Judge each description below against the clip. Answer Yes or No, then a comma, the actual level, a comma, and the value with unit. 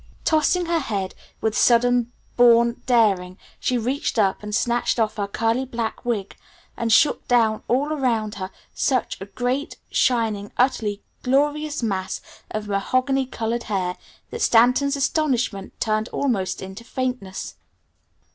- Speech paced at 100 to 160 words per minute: Yes, slow, 135 wpm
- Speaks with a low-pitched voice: No, high, 235 Hz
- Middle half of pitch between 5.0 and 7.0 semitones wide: No, average, 3.6 semitones